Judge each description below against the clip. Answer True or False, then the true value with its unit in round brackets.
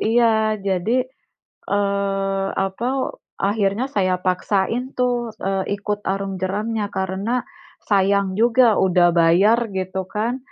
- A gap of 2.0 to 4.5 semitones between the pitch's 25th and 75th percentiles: True (2.9 semitones)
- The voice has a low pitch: False (200 Hz)